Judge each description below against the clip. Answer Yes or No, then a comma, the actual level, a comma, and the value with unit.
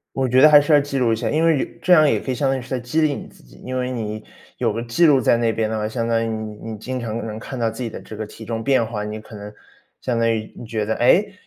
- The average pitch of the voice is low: Yes, low, 115 Hz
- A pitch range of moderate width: Yes, average, 3.3 semitones